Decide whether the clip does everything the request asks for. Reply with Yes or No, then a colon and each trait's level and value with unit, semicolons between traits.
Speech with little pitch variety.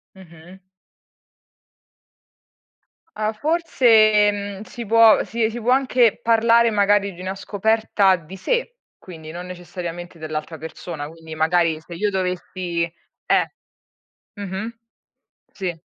No: average, 4.3 semitones